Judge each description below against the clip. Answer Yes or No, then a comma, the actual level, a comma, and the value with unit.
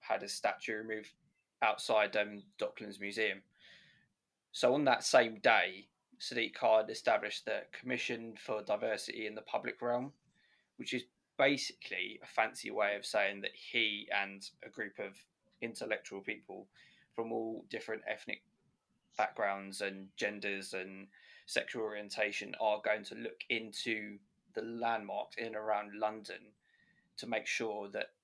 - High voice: No, low, 105 Hz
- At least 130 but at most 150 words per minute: Yes, average, 140 wpm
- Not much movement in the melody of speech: Yes, narrow, 2.0 semitones